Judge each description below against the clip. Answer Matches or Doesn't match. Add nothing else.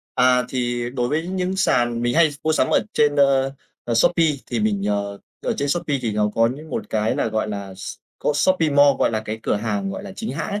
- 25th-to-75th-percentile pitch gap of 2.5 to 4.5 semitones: Doesn't match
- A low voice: Matches